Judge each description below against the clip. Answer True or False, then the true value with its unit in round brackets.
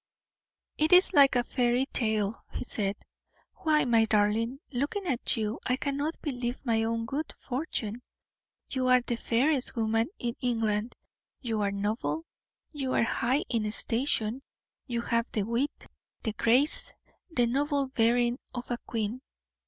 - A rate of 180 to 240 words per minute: False (145 wpm)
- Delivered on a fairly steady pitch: False (3.2 semitones)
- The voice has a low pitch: False (240 Hz)